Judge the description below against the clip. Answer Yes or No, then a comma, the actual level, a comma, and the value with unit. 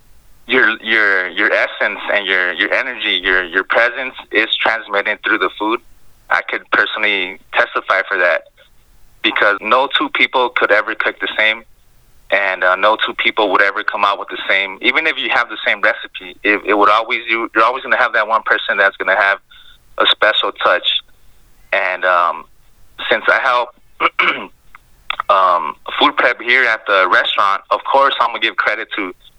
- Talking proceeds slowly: No, average, 180 wpm